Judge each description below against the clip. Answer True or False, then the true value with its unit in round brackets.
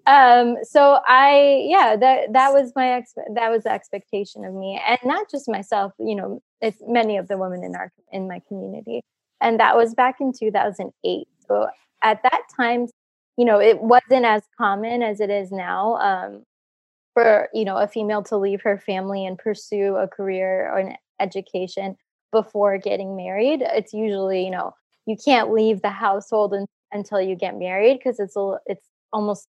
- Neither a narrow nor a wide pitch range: True (3.6 semitones)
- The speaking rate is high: False (185 wpm)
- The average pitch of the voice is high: True (210 Hz)